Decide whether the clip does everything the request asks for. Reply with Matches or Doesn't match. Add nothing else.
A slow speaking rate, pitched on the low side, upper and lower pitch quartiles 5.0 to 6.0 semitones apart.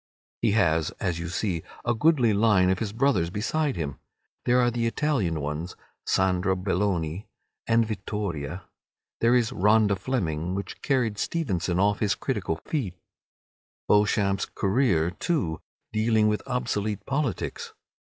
Doesn't match